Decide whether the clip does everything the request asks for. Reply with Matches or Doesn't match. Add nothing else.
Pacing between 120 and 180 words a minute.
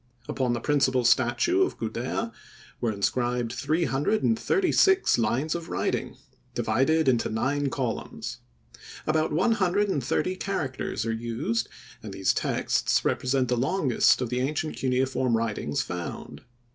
Matches